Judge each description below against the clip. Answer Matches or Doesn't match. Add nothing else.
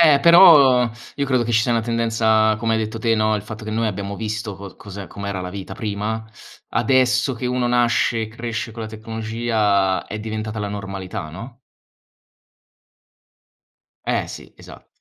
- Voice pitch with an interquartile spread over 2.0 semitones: Matches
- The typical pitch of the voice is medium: Doesn't match